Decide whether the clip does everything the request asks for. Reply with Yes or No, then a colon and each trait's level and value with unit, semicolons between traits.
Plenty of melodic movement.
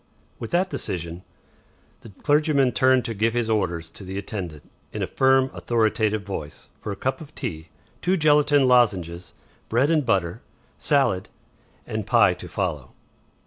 Yes: wide, 6.4 semitones